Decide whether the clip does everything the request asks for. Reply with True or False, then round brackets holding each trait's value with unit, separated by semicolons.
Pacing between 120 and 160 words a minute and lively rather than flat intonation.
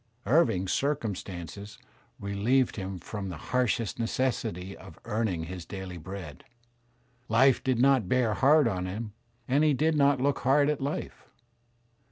True (140 wpm; 6.0 semitones)